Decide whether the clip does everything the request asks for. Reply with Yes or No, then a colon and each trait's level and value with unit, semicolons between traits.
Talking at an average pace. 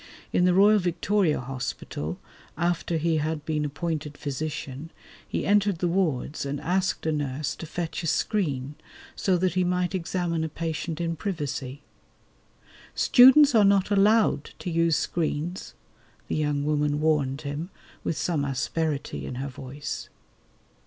Yes: average, 145 wpm